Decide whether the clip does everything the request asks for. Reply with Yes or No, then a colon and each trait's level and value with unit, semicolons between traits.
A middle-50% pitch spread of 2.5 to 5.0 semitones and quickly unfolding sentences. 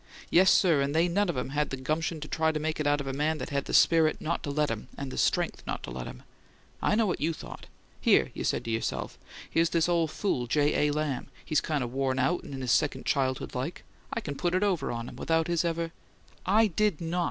Yes: average, 3.6 semitones; fast, 265 wpm